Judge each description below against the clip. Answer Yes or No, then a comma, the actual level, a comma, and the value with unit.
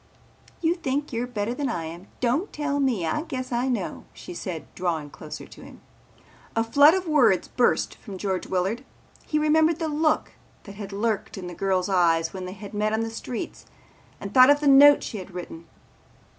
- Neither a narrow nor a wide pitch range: No, wide, 7.3 semitones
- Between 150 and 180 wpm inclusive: No, average, 200 wpm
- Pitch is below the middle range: No, high, 230 Hz